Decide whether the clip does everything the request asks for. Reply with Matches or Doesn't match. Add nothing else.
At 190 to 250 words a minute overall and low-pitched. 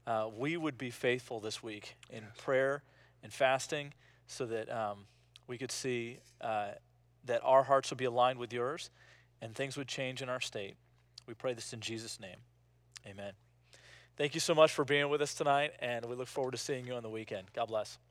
Matches